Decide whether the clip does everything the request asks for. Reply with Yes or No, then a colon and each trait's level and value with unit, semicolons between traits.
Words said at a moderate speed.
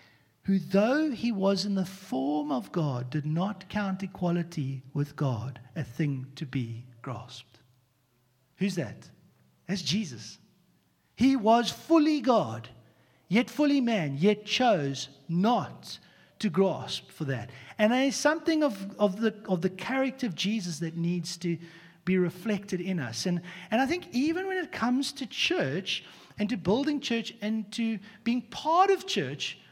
Yes: average, 155 wpm